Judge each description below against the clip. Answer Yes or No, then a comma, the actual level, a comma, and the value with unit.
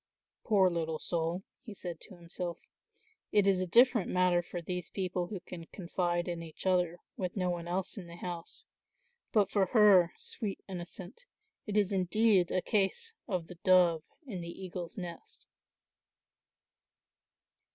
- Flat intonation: Yes, narrow, 2.2 semitones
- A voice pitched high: No, medium, 180 Hz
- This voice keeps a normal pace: Yes, average, 150 wpm